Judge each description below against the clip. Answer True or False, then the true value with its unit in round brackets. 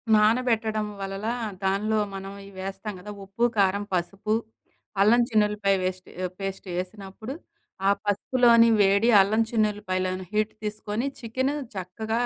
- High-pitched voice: True (210 Hz)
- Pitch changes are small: True (2.2 semitones)